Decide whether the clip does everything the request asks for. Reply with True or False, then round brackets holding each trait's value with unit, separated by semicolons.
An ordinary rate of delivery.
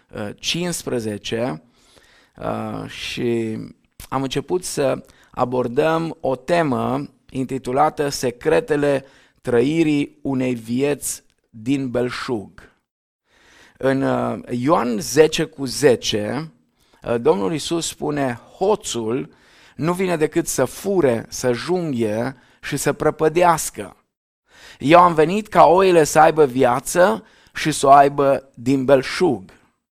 False (95 wpm)